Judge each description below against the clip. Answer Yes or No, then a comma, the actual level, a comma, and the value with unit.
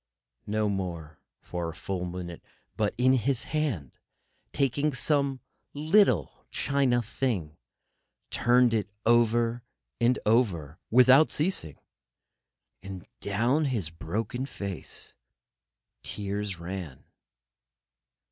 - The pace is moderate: No, slow, 90 wpm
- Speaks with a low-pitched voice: Yes, low, 110 Hz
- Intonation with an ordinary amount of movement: No, wide, 6.1 semitones